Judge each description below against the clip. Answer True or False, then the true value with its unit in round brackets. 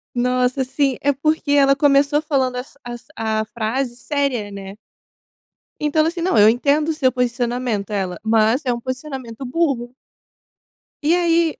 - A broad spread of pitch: False (3.3 semitones)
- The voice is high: True (255 Hz)